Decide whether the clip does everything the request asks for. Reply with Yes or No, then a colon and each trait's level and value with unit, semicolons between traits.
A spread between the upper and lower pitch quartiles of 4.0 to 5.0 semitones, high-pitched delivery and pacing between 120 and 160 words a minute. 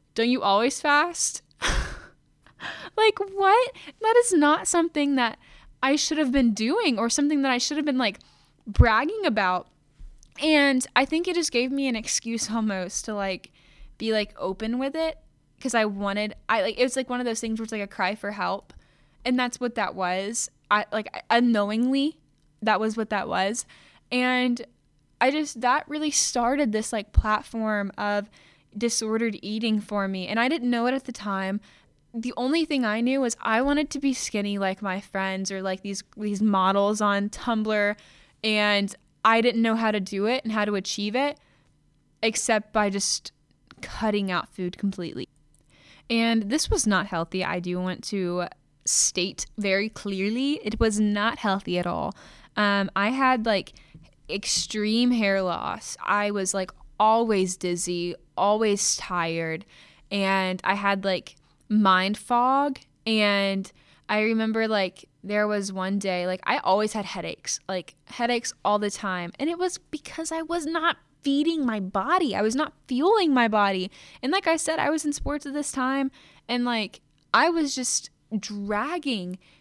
No: average, 4.6 semitones; high, 220 Hz; average, 170 wpm